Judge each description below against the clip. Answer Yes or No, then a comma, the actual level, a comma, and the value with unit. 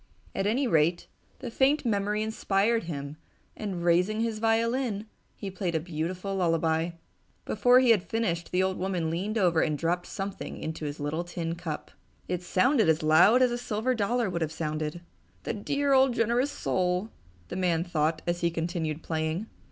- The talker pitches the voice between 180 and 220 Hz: Yes, medium, 185 Hz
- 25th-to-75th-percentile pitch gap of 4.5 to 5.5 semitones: Yes, average, 5.2 semitones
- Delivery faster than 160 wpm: Yes, average, 175 wpm